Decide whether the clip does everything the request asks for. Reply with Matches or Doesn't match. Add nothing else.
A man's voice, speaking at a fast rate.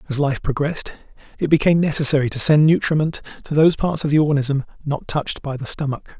Doesn't match